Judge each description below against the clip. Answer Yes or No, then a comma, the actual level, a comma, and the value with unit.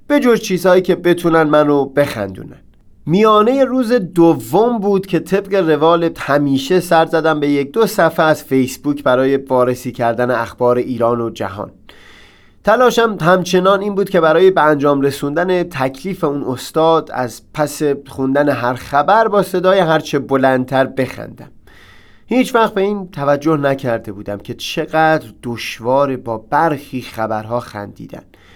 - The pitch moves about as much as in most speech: No, wide, 6.2 semitones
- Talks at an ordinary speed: Yes, average, 140 wpm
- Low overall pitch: No, medium, 145 Hz